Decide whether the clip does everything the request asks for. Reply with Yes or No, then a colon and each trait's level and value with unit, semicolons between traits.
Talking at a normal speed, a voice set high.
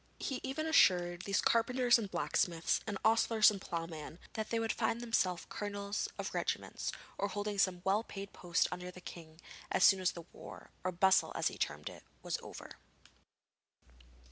Yes: average, 170 wpm; high, 200 Hz